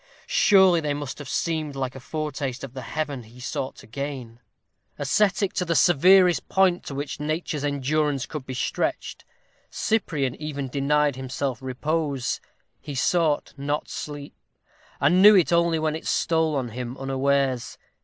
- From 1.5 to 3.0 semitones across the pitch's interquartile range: No, average, 3.4 semitones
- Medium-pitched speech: Yes, medium, 145 Hz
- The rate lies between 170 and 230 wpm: No, average, 155 wpm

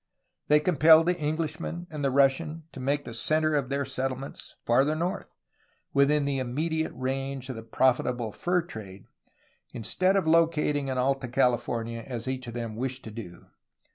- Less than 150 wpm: No, average, 170 wpm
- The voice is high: No, low, 135 Hz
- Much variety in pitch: No, average, 4.0 semitones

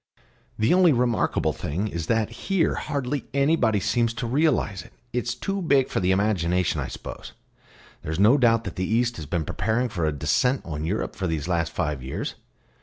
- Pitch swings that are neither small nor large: No, wide, 6.7 semitones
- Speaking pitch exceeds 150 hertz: No, low, 110 Hz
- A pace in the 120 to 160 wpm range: No, average, 190 wpm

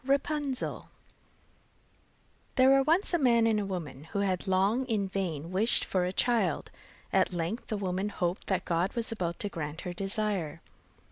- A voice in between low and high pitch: No, high, 195 Hz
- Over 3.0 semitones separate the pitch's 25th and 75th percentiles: Yes, average, 4.7 semitones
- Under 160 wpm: No, average, 165 wpm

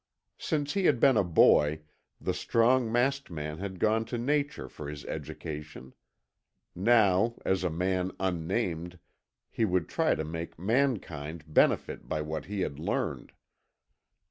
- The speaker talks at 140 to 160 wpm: Yes, average, 145 wpm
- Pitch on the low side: Yes, very low, 95 Hz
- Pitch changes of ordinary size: No, wide, 6.7 semitones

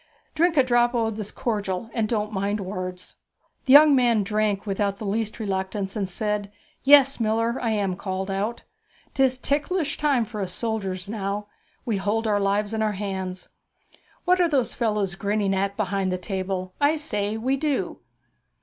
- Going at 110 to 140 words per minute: No, average, 170 wpm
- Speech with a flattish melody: No, average, 3.4 semitones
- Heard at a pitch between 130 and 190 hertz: No, high, 210 Hz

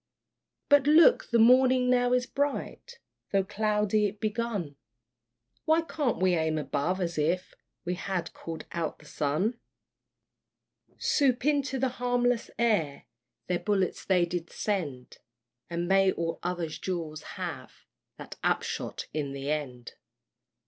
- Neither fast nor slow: No, slow, 130 wpm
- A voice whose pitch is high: Yes, high, 195 Hz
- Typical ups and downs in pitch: No, wide, 6.9 semitones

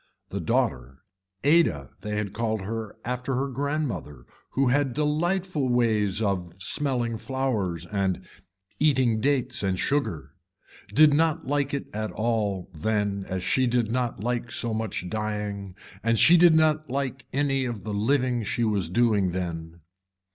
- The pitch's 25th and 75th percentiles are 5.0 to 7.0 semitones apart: Yes, wide, 5.5 semitones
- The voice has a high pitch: No, low, 115 Hz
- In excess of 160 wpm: No, average, 145 wpm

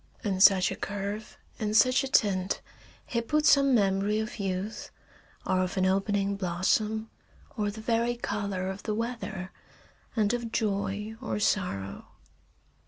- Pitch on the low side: No, high, 205 Hz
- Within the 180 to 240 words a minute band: No, average, 145 wpm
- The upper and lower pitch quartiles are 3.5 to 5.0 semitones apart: No, average, 2.7 semitones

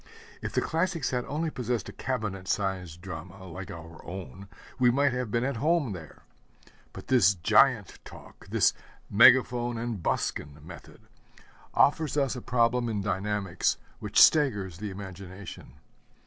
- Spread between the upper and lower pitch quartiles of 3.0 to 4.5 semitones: No, average, 4.9 semitones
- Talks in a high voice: No, low, 110 Hz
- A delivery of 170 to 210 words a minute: No, average, 145 wpm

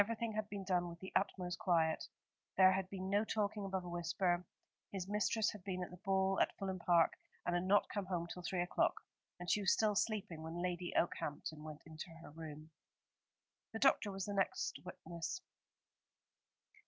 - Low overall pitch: No, medium, 185 Hz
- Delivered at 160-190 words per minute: Yes, average, 185 wpm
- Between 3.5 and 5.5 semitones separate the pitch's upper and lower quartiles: No, narrow, 2.5 semitones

